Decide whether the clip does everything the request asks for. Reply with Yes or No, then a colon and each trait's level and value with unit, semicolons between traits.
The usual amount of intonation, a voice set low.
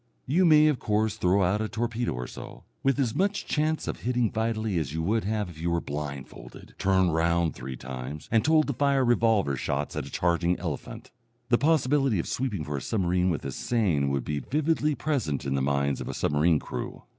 No: wide, 8.5 semitones; low, 100 Hz